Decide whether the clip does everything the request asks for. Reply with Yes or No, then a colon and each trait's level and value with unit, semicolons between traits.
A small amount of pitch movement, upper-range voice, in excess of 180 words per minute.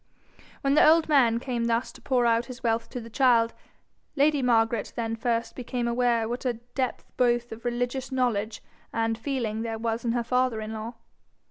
Yes: narrow, 1.7 semitones; high, 235 Hz; average, 190 wpm